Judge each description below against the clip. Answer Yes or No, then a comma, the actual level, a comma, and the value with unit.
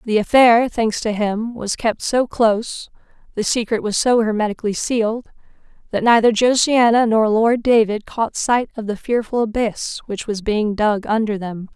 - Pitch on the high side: Yes, high, 220 Hz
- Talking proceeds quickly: No, average, 170 wpm